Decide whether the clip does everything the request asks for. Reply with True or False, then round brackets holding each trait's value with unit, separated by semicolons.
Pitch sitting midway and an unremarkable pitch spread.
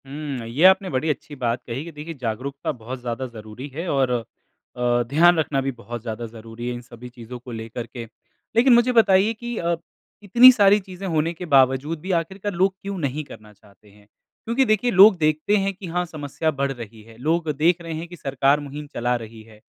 False (145 Hz; 6.7 semitones)